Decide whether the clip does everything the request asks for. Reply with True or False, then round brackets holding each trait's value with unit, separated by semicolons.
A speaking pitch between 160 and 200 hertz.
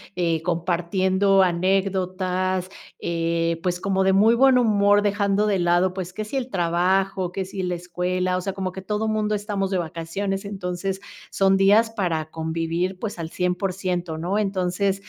True (190 Hz)